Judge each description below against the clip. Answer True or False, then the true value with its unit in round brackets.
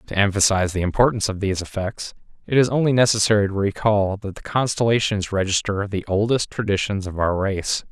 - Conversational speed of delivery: True (175 wpm)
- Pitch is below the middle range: True (100 Hz)